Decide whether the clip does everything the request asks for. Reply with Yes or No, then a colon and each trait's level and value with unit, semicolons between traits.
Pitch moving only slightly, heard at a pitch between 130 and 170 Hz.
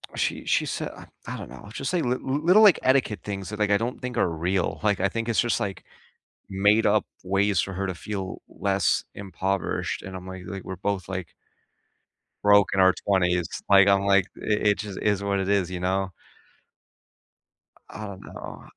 No: narrow, 1.9 semitones; low, 100 Hz